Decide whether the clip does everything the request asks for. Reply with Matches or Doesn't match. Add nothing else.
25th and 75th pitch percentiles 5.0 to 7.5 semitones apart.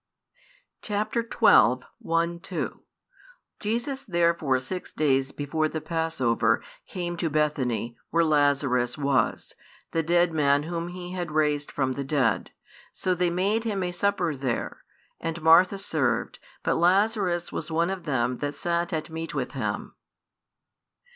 Doesn't match